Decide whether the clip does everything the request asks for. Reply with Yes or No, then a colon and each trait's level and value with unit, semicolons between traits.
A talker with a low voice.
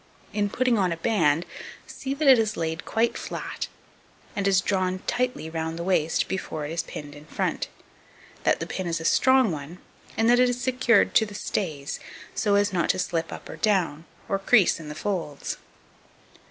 No: high, 190 Hz